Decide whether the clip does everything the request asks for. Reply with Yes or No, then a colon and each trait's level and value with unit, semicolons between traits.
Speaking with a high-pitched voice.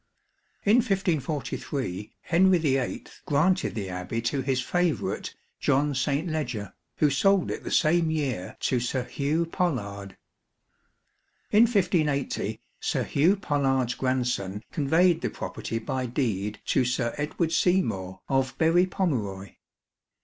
No: medium, 140 Hz